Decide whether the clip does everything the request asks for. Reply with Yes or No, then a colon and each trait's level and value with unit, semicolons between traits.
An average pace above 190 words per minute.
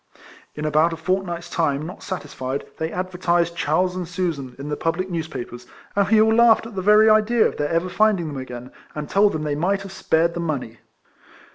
Yes: fast, 205 wpm